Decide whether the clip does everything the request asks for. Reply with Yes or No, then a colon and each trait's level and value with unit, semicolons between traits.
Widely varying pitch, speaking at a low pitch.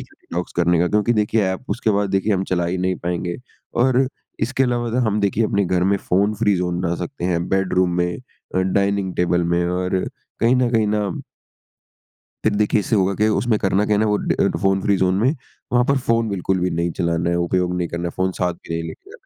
No: average, 3.3 semitones; very low, 95 Hz